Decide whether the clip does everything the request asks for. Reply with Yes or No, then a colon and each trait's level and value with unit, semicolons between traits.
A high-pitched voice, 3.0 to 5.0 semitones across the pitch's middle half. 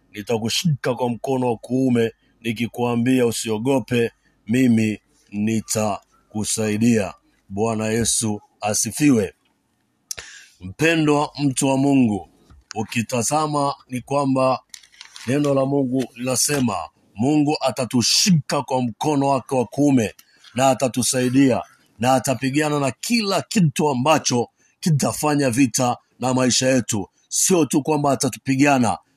No: low, 130 Hz; average, 3.6 semitones